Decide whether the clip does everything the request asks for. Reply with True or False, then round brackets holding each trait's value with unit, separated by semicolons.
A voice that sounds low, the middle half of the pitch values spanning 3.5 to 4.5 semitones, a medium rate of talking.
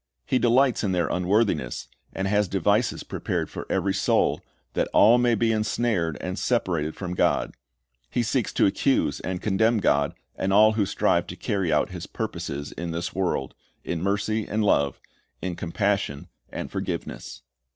True (100 Hz; 4.2 semitones; 160 wpm)